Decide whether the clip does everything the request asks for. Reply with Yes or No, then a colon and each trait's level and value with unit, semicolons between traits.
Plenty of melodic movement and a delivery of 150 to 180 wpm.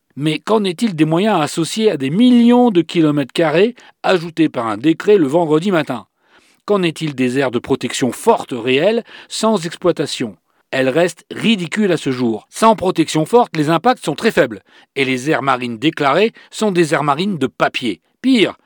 Yes: wide, 6.9 semitones; average, 175 wpm